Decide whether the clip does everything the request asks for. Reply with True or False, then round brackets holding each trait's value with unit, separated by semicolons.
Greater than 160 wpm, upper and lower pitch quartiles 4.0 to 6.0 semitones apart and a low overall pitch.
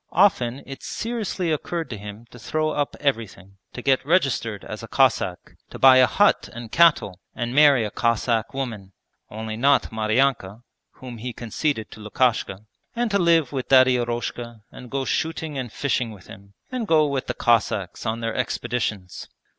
True (170 wpm; 4.5 semitones; 125 Hz)